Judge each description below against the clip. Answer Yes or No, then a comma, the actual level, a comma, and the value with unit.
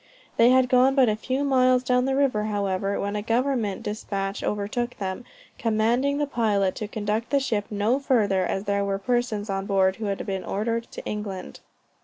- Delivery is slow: No, average, 190 wpm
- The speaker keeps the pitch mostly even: No, average, 3.8 semitones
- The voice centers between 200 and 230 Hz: Yes, high, 215 Hz